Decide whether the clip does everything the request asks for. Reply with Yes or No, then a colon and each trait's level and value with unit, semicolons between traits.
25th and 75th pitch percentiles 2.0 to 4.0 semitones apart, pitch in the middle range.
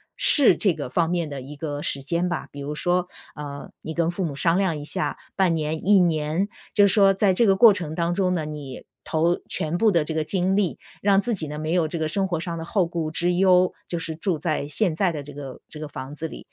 Yes: average, 3.3 semitones; medium, 170 Hz